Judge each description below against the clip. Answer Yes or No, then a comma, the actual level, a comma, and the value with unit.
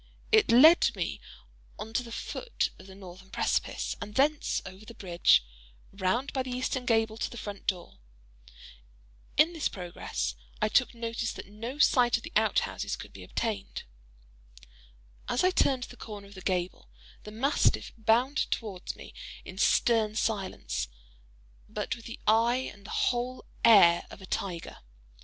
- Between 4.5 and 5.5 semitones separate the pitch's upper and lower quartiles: No, average, 4.1 semitones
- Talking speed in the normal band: Yes, average, 160 wpm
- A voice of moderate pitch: No, high, 225 Hz